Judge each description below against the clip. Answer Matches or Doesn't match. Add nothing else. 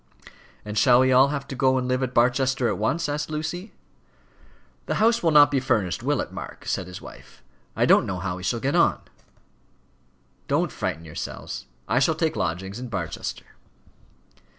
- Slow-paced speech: Doesn't match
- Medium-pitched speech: Doesn't match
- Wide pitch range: Matches